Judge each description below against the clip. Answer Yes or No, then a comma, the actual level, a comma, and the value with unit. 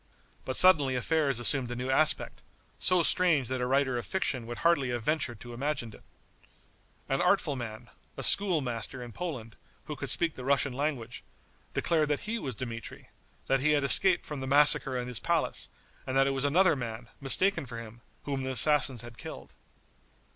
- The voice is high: No, low, 135 Hz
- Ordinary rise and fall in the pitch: Yes, average, 3.8 semitones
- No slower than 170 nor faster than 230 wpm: Yes, average, 185 wpm